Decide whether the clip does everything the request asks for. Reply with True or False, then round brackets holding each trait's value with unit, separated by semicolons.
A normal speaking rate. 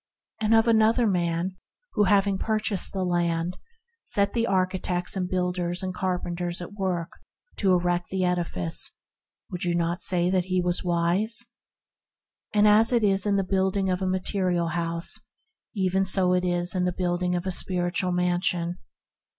True (160 wpm)